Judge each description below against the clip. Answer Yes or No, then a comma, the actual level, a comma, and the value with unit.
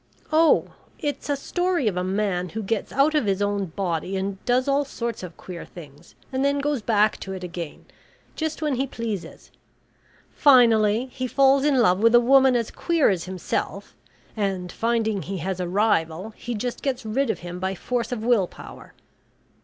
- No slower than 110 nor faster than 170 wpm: No, average, 185 wpm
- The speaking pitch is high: Yes, high, 220 Hz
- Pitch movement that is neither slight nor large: No, wide, 5.8 semitones